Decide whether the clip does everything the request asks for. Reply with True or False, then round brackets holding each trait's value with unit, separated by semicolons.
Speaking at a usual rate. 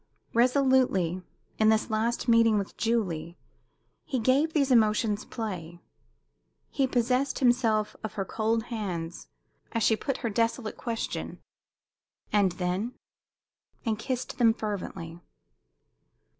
False (115 wpm)